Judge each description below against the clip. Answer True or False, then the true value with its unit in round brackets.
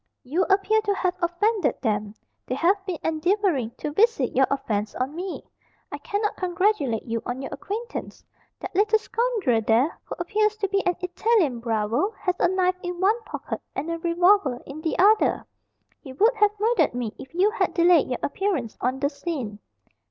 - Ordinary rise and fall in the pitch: False (7.5 semitones)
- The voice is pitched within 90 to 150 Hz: False (350 Hz)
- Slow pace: False (180 wpm)